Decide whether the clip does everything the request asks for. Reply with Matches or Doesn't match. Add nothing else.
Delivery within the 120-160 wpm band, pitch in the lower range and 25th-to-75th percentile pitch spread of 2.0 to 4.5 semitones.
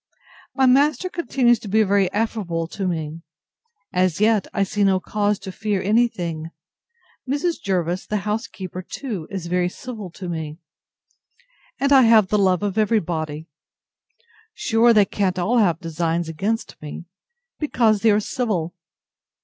Doesn't match